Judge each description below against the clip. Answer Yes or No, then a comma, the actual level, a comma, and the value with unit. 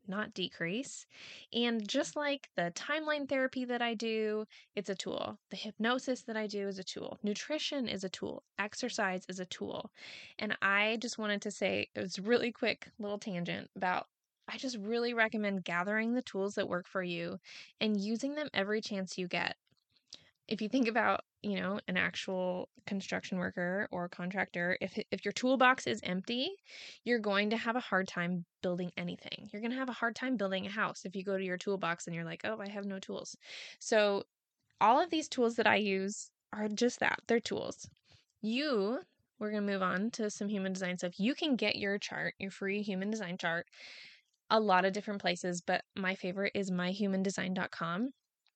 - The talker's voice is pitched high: Yes, high, 205 Hz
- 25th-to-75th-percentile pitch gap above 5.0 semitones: No, average, 3.6 semitones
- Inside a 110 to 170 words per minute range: No, average, 195 wpm